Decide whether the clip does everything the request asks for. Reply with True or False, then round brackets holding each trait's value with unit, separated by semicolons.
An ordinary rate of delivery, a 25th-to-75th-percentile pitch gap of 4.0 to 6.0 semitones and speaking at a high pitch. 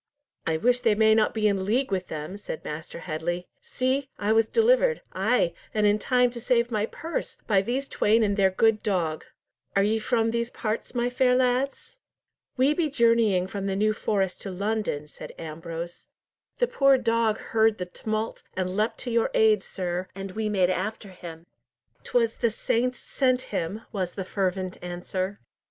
True (175 wpm; 4.3 semitones; 215 Hz)